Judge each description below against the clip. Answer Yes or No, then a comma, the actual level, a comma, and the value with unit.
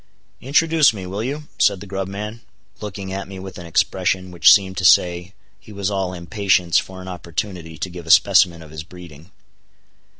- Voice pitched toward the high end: No, very low, 95 Hz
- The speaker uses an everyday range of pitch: No, narrow, 2.3 semitones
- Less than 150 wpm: No, average, 190 wpm